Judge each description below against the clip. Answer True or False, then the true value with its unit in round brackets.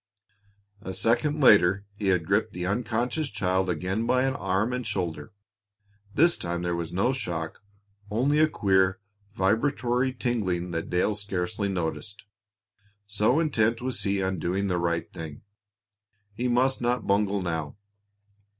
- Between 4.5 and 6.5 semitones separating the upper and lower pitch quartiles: True (5.2 semitones)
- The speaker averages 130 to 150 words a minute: True (140 wpm)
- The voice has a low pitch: True (100 Hz)